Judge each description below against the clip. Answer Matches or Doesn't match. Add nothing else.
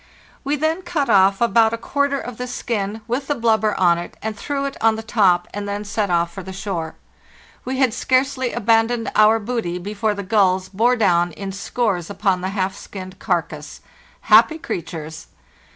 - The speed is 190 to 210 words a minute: Matches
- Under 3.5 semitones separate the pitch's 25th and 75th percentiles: Doesn't match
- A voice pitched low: Doesn't match